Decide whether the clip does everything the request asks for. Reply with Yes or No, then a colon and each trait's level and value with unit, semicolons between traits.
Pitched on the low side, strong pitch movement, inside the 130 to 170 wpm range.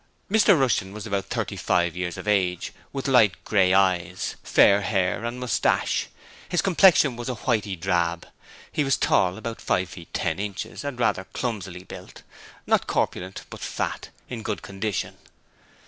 No: low, 100 Hz; average, 4.7 semitones; average, 165 wpm